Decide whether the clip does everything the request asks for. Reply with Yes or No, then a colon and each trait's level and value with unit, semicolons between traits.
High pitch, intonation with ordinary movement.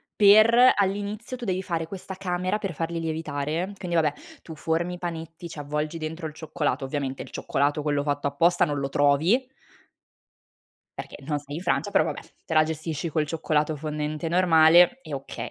No: medium, 160 Hz; average, 3.1 semitones